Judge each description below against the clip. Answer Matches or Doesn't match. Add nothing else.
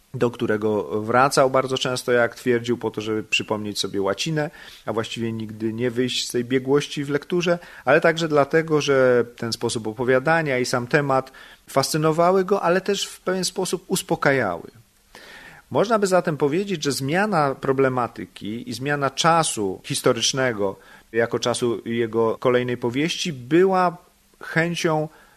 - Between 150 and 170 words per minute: Doesn't match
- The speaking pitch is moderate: Doesn't match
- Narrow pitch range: Doesn't match